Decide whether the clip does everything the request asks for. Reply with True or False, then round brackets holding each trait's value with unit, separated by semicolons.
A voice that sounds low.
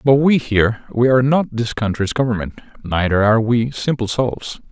True (115 Hz)